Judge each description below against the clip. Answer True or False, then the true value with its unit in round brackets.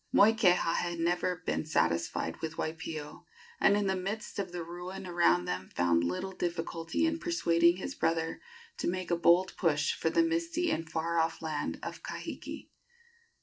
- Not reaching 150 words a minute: False (165 wpm)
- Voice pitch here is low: False (170 Hz)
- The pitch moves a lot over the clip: False (2.9 semitones)